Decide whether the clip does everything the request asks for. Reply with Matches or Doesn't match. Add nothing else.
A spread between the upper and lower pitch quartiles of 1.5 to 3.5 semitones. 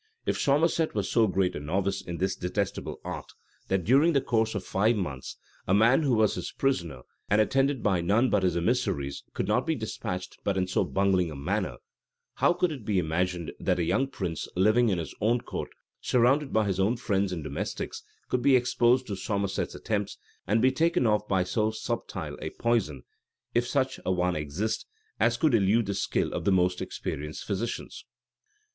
Doesn't match